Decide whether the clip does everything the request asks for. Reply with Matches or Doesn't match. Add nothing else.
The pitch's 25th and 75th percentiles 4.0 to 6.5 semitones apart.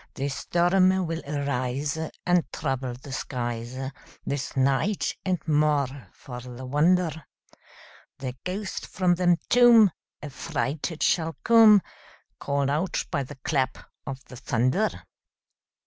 Matches